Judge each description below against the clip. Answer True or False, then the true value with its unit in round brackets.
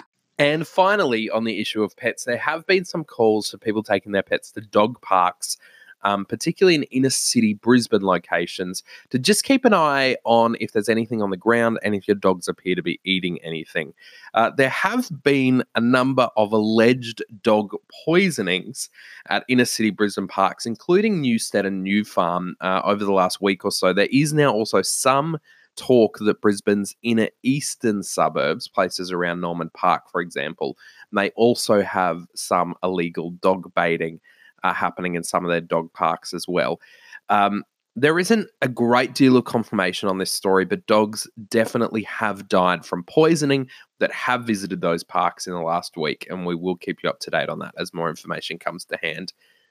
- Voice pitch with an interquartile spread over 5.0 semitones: True (5.5 semitones)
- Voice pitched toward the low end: True (110 Hz)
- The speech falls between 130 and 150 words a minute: False (185 wpm)